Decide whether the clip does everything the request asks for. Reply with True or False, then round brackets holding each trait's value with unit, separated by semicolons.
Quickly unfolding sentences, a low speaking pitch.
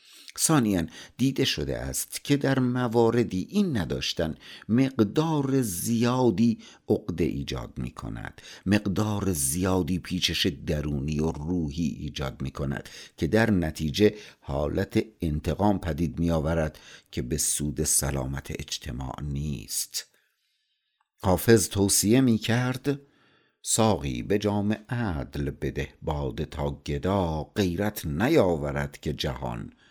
False (110 wpm; 90 Hz)